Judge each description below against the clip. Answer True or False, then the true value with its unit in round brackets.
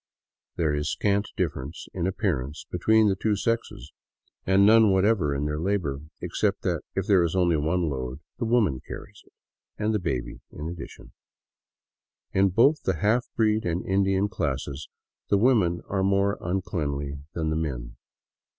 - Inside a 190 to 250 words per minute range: False (160 wpm)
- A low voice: True (90 Hz)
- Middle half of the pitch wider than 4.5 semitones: True (5.3 semitones)